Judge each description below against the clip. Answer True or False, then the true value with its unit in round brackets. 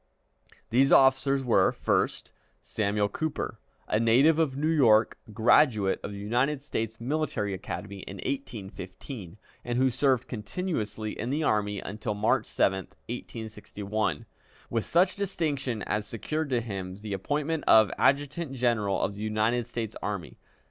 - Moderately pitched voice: False (115 Hz)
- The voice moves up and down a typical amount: True (4.9 semitones)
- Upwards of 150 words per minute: False (140 wpm)